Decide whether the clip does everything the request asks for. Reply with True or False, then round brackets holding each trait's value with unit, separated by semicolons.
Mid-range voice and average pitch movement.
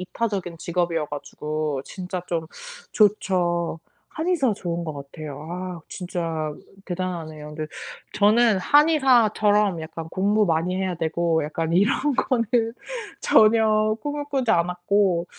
True (180 Hz; 4.7 semitones)